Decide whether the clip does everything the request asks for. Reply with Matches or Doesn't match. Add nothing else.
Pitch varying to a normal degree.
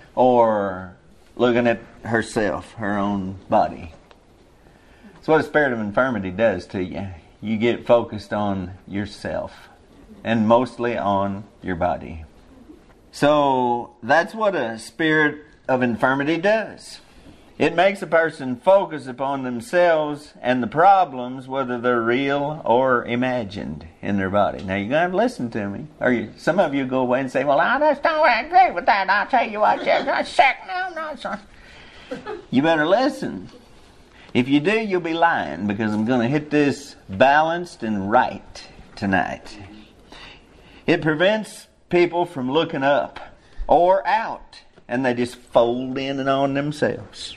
Doesn't match